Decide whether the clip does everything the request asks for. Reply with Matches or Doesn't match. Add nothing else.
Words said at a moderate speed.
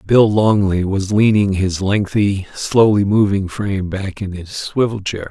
Matches